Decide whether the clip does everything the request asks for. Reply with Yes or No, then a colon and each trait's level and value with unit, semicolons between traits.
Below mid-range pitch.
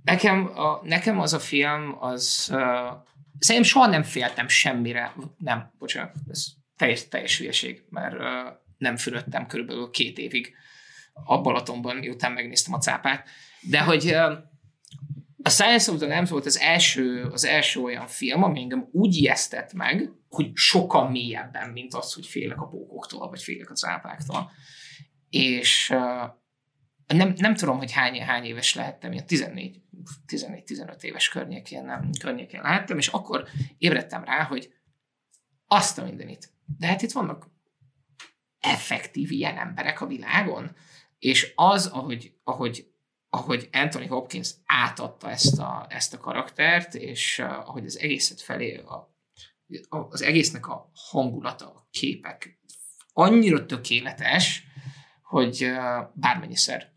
No: medium, 145 Hz